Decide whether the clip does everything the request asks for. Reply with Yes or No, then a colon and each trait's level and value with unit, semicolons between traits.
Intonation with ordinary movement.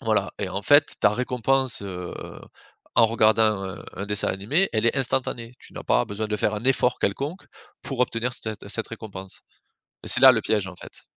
Yes: average, 3.6 semitones